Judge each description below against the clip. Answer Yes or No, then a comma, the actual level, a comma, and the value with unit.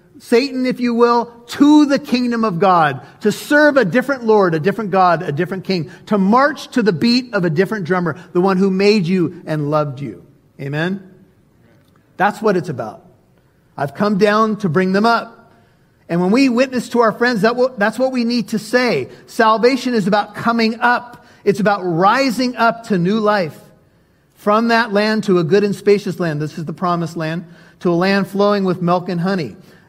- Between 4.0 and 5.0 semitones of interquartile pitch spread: Yes, average, 4.7 semitones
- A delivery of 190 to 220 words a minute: Yes, average, 195 wpm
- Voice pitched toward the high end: Yes, high, 205 Hz